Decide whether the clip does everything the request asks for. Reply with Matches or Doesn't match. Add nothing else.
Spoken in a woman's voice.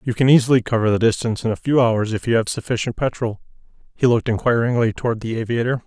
Doesn't match